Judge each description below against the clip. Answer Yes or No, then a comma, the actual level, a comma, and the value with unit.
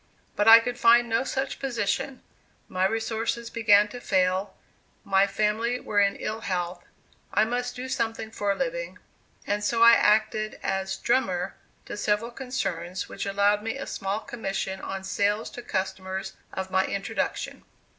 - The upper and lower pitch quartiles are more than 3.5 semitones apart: No, average, 3.2 semitones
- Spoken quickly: No, average, 155 wpm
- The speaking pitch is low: No, high, 210 Hz